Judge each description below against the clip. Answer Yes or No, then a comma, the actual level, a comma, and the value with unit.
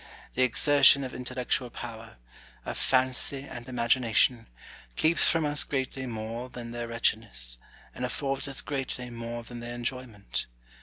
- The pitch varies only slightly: Yes, narrow, 2.1 semitones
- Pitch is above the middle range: No, low, 125 Hz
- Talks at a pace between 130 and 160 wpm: Yes, average, 140 wpm